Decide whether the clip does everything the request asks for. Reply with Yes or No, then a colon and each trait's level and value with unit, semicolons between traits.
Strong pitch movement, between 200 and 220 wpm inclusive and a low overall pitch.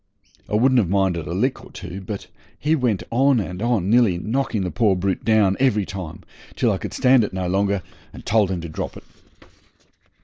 No: average, 4.3 semitones; fast, 205 wpm; low, 100 Hz